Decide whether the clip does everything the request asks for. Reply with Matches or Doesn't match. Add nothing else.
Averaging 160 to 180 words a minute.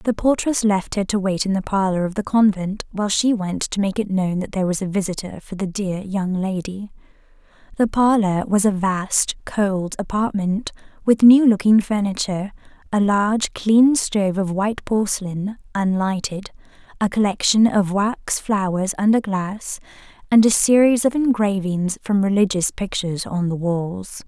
Matches